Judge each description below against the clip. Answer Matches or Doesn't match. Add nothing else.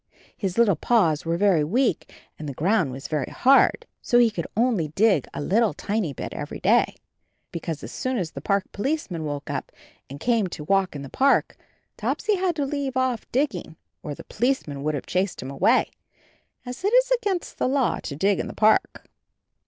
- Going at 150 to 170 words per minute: Doesn't match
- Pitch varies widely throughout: Matches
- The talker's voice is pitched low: Doesn't match